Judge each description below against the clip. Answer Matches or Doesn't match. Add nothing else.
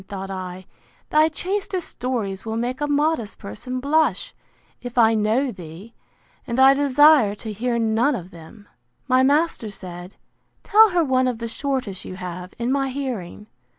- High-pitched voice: Matches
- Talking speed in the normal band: Matches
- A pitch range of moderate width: Doesn't match